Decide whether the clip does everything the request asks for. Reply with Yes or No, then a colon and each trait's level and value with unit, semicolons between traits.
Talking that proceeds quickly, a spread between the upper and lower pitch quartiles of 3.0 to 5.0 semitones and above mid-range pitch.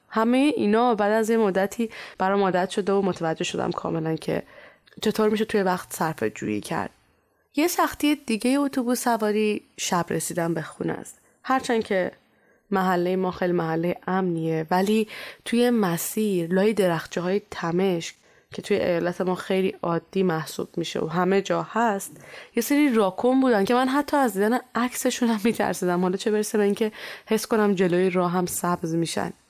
Yes: fast, 165 wpm; average, 4.1 semitones; high, 195 Hz